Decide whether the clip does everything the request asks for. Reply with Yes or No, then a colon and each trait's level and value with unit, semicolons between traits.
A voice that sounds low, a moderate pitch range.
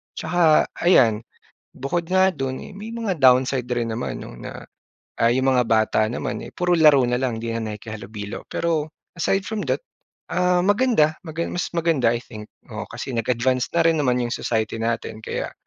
No: low, 130 Hz; wide, 6.5 semitones